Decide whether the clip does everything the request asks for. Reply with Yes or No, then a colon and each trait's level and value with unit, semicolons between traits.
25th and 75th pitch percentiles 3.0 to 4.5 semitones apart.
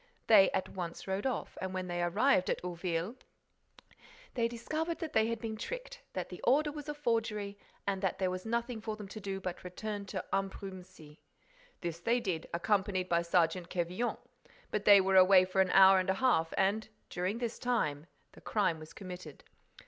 Yes: average, 3.9 semitones